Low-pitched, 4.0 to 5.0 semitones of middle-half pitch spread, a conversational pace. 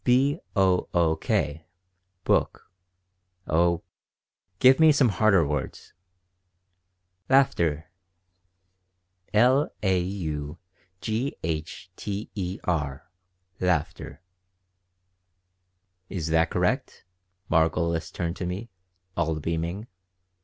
No: very low, 90 Hz; average, 4.5 semitones; slow, 90 wpm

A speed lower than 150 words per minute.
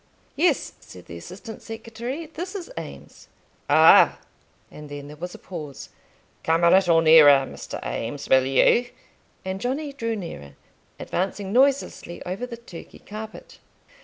Yes: average, 140 wpm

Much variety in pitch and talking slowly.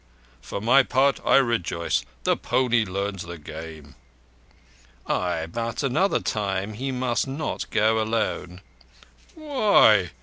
Yes: wide, 6.0 semitones; slow, 115 wpm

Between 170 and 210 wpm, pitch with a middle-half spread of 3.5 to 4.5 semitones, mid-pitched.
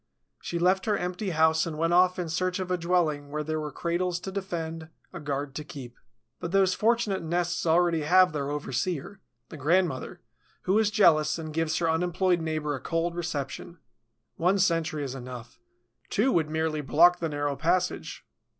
No: average, 180 wpm; average, 3.0 semitones; medium, 165 Hz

